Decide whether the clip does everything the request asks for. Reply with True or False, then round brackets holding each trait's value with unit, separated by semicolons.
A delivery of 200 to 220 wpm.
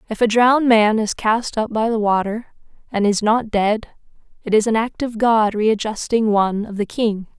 True (205 wpm)